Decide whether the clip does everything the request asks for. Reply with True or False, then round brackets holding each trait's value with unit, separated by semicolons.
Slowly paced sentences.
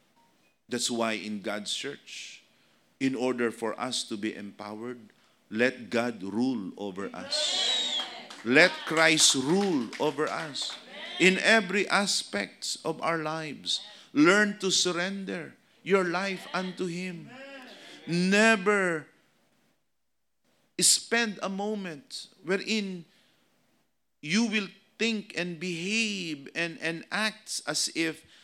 True (105 wpm)